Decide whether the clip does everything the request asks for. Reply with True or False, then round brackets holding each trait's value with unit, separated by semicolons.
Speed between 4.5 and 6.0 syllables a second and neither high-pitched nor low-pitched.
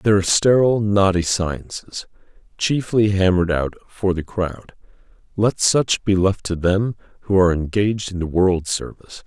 False (5.0 syllables/s; 95 Hz)